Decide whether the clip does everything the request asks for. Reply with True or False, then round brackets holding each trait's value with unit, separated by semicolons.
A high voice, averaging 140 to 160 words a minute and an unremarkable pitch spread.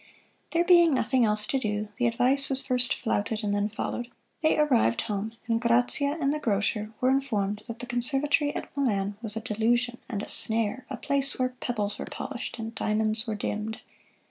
False (235 Hz; 190 wpm; 3.8 semitones)